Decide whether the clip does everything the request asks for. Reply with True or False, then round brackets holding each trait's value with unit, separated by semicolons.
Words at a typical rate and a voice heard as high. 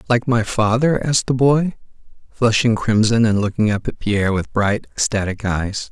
False (175 wpm; 110 Hz)